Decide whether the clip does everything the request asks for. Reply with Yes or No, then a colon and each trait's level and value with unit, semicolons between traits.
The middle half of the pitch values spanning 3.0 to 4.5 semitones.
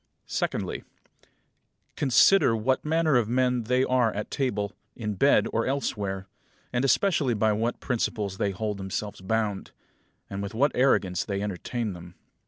Yes: average, 4.2 semitones